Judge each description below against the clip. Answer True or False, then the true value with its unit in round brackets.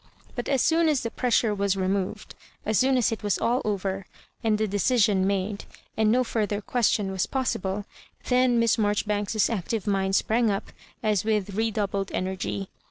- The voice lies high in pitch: True (210 Hz)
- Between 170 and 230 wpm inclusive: True (175 wpm)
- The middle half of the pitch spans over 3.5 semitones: False (2.8 semitones)